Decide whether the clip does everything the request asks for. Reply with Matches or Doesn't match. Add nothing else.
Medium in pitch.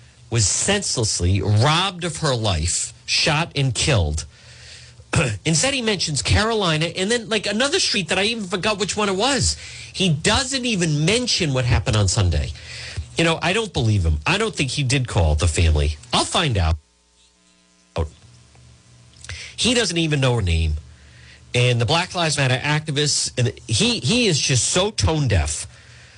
Doesn't match